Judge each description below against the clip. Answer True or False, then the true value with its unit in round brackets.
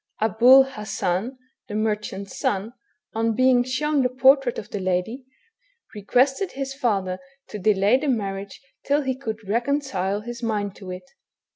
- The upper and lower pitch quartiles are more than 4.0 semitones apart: True (4.5 semitones)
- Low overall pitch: False (225 Hz)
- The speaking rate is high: False (150 wpm)